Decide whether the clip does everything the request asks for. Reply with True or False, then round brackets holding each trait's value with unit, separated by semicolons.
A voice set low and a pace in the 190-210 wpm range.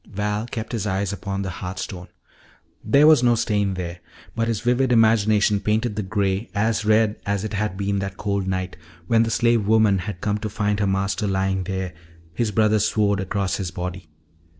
True (105 Hz; 195 wpm)